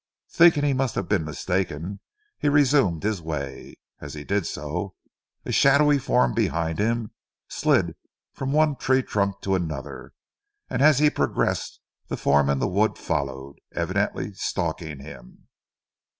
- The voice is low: Yes, very low, 95 Hz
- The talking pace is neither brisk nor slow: Yes, average, 145 wpm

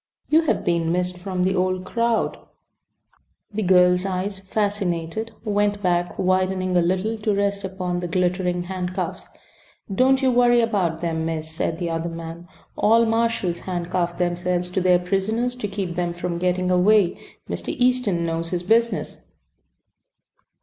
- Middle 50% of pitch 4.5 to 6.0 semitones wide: No, average, 2.7 semitones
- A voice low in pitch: No, medium, 185 Hz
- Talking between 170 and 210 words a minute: No, average, 150 wpm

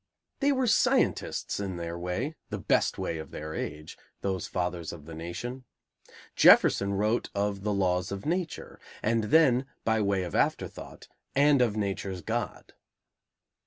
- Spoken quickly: No, average, 150 wpm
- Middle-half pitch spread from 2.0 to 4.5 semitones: No, wide, 5.6 semitones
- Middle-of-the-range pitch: No, low, 100 Hz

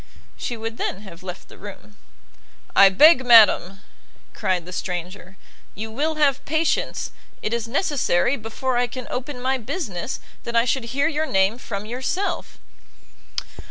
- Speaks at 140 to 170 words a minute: Yes, average, 150 wpm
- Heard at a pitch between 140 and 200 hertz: No, high, 230 Hz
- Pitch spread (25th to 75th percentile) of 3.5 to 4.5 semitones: No, average, 5.1 semitones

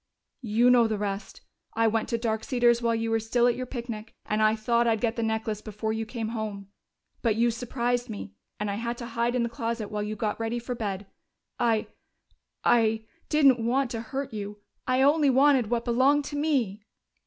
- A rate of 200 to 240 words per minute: Yes, fast, 205 wpm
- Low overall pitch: No, high, 230 Hz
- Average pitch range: No, narrow, 1.9 semitones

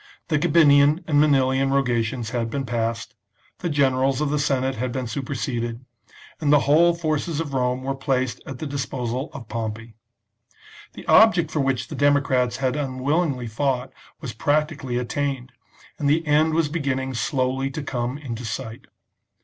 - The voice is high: No, low, 135 Hz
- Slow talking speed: No, average, 155 wpm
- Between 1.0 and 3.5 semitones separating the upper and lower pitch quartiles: Yes, average, 2.8 semitones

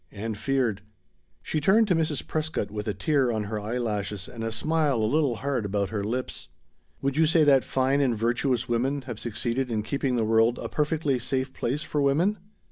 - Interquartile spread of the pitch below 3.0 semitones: No, average, 4.5 semitones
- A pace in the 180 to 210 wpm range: Yes, average, 200 wpm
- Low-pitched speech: Yes, low, 125 Hz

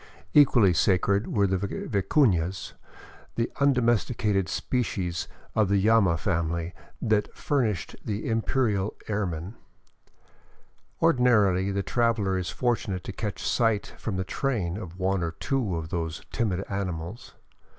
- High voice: No, low, 100 Hz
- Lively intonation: No, average, 3.9 semitones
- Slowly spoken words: Yes, slow, 125 wpm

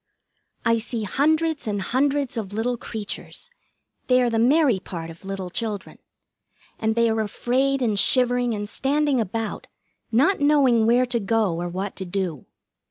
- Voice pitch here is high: Yes, high, 230 Hz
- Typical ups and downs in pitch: Yes, average, 4.2 semitones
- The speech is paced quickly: No, average, 160 wpm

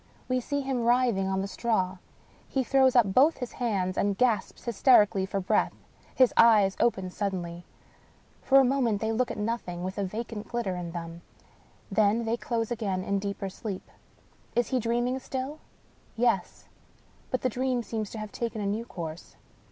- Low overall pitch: No, high, 220 Hz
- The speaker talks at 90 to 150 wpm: No, average, 175 wpm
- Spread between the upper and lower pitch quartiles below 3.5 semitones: No, average, 4.1 semitones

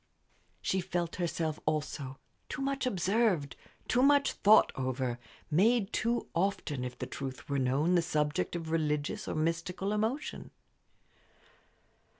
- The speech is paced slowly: Yes, slow, 130 wpm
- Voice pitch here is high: No, medium, 165 Hz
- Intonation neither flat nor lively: No, wide, 5.9 semitones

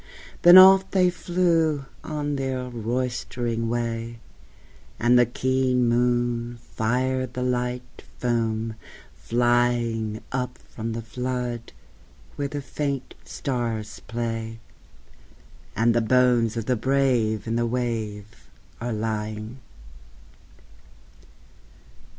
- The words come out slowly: Yes, slow, 100 wpm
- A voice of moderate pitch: No, low, 120 Hz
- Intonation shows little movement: Yes, narrow, 2.0 semitones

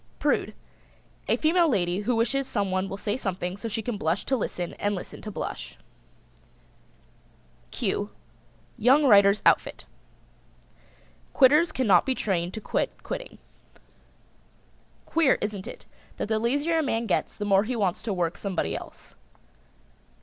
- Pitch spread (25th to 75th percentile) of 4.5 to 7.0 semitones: Yes, average, 5.1 semitones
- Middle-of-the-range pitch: No, high, 210 Hz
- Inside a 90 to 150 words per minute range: Yes, average, 145 wpm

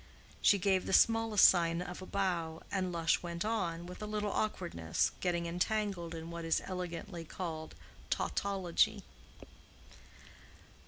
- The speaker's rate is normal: No, slow, 130 wpm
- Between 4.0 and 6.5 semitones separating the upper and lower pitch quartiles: No, average, 2.8 semitones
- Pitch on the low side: No, medium, 180 Hz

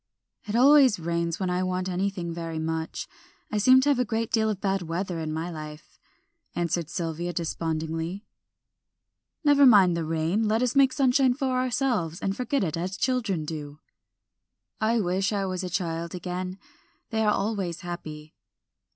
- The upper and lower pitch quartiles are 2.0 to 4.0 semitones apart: No, average, 5.1 semitones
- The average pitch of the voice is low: No, medium, 185 Hz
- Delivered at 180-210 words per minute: No, average, 165 wpm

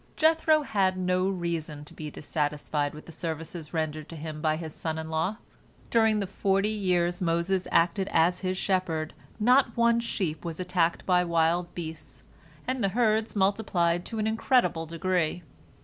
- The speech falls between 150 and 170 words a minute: Yes, average, 165 wpm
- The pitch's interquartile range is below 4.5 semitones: Yes, average, 3.9 semitones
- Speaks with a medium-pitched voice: Yes, medium, 175 Hz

